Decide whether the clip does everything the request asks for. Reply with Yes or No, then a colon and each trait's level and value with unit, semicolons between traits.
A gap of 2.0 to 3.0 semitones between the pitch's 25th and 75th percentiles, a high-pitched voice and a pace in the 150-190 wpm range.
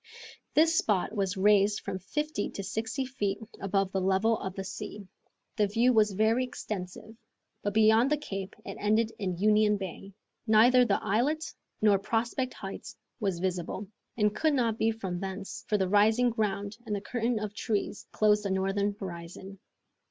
Yes: narrow, 2.6 semitones; high, 210 Hz; average, 165 wpm